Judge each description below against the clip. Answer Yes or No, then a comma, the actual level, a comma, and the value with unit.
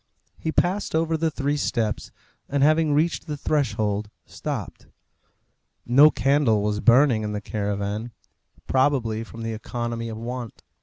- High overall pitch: No, low, 120 Hz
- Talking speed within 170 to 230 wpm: No, average, 140 wpm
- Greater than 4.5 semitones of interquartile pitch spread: Yes, average, 5.2 semitones